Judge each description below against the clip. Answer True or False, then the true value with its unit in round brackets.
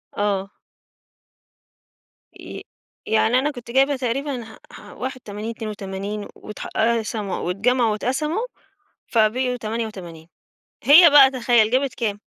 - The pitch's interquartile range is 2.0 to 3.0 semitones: False (3.6 semitones)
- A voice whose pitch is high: True (230 Hz)